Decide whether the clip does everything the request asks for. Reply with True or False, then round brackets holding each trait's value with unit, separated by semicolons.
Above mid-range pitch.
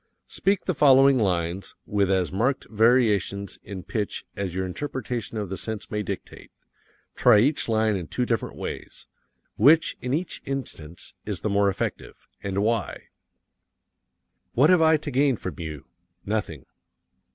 False (110 Hz)